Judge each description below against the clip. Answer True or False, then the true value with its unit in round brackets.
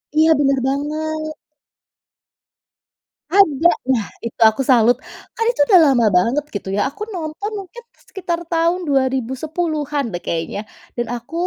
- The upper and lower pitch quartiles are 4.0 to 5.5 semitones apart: True (4.8 semitones)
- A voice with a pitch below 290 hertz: False (295 Hz)